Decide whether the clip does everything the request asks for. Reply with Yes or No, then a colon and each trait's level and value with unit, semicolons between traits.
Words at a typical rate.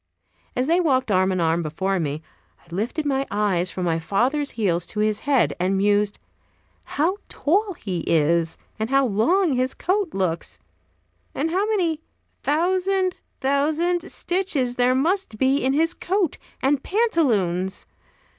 Yes: average, 145 wpm